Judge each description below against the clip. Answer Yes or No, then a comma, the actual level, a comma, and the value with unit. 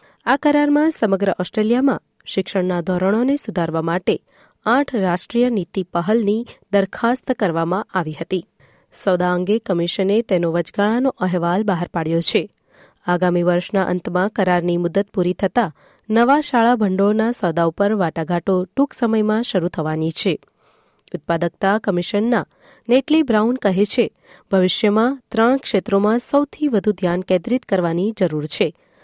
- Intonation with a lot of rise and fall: No, average, 4.5 semitones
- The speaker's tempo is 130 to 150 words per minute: No, average, 120 wpm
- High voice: Yes, high, 195 Hz